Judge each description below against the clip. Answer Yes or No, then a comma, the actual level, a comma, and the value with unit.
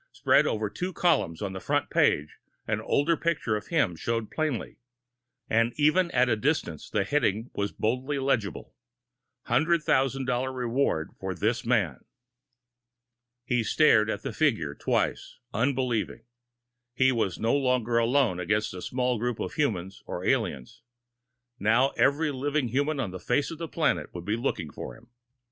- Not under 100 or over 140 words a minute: No, average, 155 wpm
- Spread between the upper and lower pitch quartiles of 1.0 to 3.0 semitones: No, average, 5.1 semitones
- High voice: No, low, 120 Hz